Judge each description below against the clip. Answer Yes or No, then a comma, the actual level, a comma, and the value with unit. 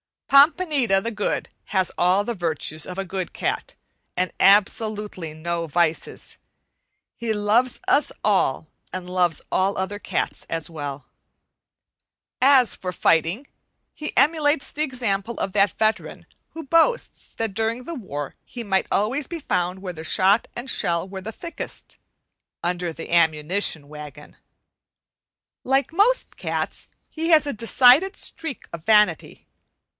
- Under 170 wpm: Yes, average, 140 wpm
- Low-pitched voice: No, high, 200 Hz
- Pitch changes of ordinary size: No, wide, 6.5 semitones